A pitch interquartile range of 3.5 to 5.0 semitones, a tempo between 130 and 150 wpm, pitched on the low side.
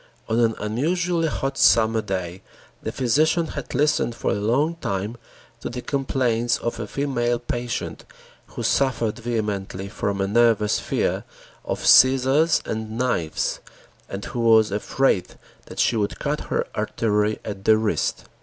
Yes: average, 3.9 semitones; average, 145 wpm; low, 115 Hz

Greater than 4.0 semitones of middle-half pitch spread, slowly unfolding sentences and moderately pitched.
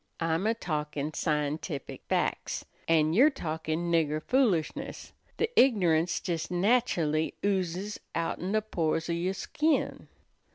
Yes: average, 4.4 semitones; slow, 120 wpm; medium, 170 Hz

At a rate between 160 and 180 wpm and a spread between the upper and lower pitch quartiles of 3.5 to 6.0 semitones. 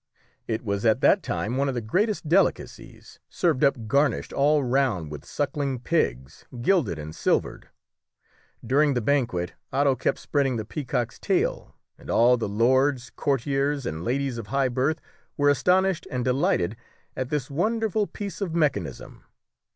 No: average, 150 wpm; average, 4.2 semitones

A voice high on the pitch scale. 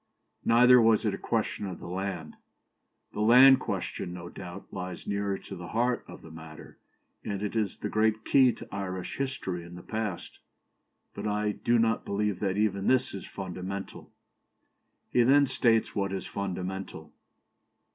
No: low, 100 Hz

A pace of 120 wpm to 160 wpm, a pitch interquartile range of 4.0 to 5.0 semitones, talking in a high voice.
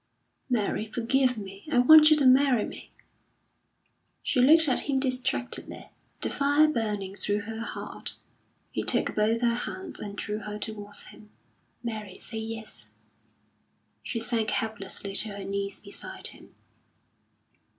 No: average, 140 wpm; average, 3.6 semitones; high, 225 Hz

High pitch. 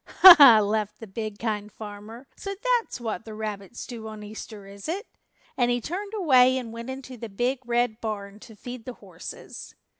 Yes: high, 225 Hz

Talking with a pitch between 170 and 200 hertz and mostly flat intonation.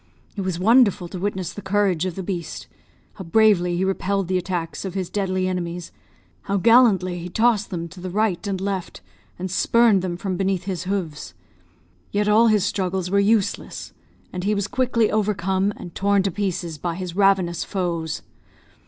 Yes: high, 190 Hz; narrow, 2.3 semitones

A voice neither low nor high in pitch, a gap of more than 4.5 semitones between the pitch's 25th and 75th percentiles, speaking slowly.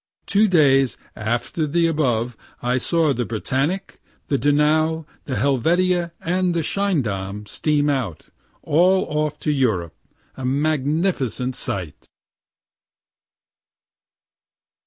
Yes: medium, 145 Hz; average, 4.9 semitones; slow, 100 wpm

